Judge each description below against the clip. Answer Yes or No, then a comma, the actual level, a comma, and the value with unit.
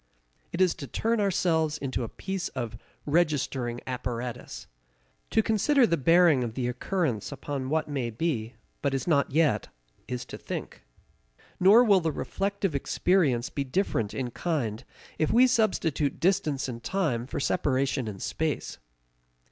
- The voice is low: No, medium, 145 Hz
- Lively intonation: Yes, wide, 6.2 semitones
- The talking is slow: No, average, 150 wpm